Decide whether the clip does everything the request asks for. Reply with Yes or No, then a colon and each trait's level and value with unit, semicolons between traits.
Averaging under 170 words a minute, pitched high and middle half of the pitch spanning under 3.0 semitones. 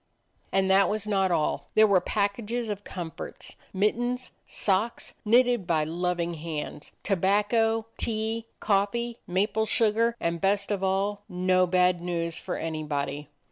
No: slow, 135 wpm; high, 195 Hz; average, 3.8 semitones